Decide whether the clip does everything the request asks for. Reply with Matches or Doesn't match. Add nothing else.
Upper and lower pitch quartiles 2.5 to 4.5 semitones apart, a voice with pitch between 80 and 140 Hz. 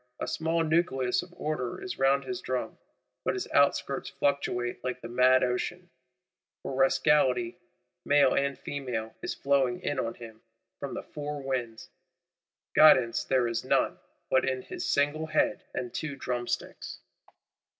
Matches